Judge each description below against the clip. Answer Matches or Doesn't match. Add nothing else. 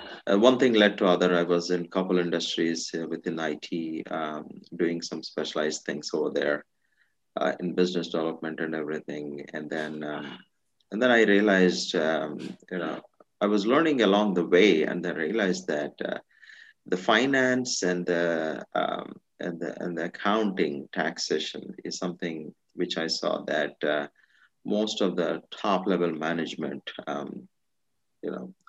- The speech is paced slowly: Doesn't match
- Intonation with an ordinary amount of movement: Matches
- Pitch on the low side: Matches